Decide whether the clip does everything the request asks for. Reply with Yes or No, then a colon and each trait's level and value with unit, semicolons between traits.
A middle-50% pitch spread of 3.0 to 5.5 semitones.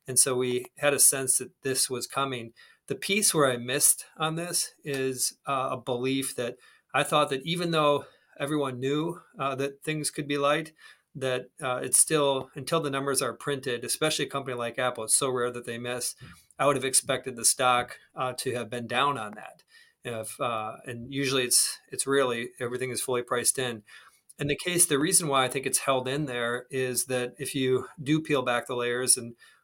No: narrow, 2.5 semitones